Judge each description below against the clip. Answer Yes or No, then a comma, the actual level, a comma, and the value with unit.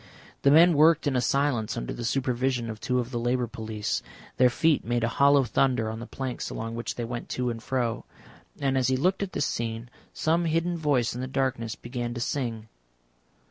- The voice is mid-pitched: No, low, 125 Hz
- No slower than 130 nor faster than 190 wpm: No, fast, 205 wpm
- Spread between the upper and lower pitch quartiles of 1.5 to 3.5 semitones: Yes, average, 3.0 semitones